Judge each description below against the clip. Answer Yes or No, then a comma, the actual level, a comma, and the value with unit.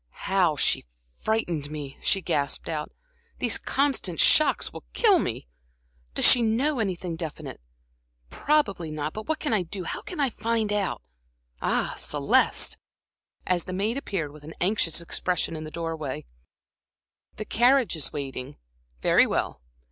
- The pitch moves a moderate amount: No, wide, 6.4 semitones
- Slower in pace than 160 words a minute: Yes, average, 150 wpm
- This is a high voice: No, medium, 180 Hz